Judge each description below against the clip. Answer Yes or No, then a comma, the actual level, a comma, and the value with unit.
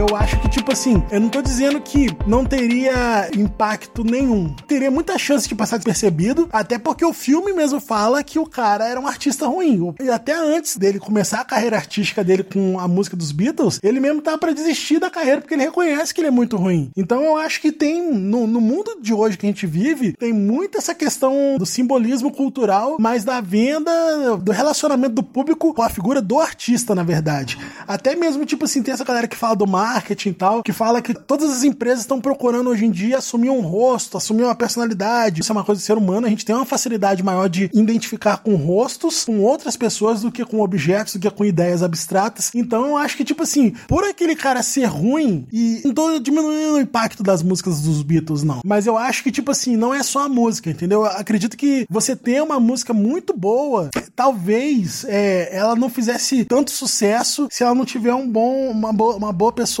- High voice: Yes, high, 235 Hz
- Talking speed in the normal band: No, fast, 215 wpm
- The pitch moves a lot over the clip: No, average, 4.9 semitones